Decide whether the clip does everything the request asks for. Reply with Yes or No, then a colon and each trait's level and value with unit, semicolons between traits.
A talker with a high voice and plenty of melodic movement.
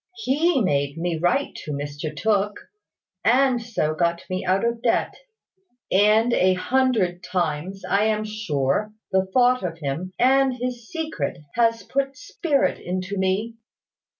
Yes: high, 210 Hz; wide, 5.9 semitones